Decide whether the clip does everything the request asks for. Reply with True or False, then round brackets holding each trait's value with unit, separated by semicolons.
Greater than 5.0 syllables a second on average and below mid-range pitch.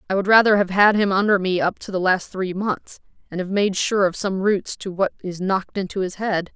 False (5.4 syllables/s; 190 Hz)